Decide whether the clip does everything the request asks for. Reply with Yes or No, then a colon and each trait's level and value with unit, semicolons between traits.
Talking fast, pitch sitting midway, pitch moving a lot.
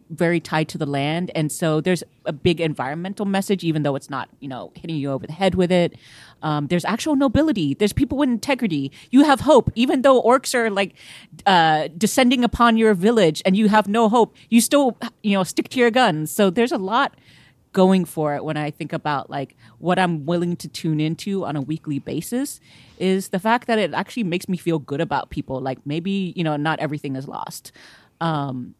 Yes: fast, 215 wpm; medium, 175 Hz; wide, 6.5 semitones